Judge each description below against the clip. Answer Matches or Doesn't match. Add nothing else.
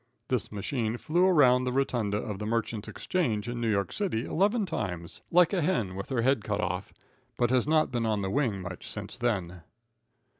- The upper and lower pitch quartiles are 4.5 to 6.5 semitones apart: Matches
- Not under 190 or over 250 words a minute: Matches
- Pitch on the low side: Matches